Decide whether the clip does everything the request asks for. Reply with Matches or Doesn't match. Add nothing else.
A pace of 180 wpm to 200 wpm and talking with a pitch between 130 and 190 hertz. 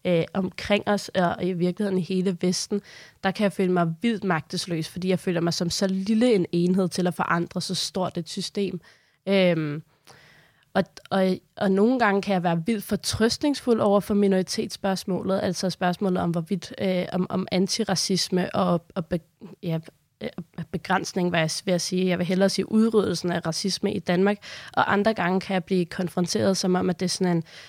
Matches